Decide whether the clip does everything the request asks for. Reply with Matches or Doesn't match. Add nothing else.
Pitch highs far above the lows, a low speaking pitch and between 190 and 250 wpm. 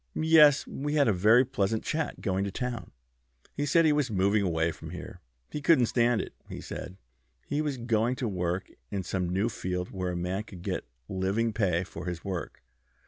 Matches